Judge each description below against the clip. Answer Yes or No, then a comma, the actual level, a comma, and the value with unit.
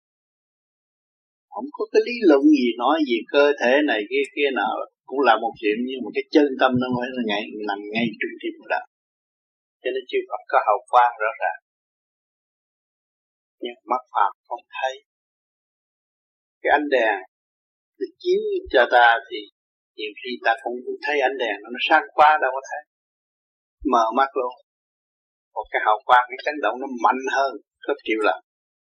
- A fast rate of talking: No, average, 175 wpm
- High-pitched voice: Yes, high, 205 Hz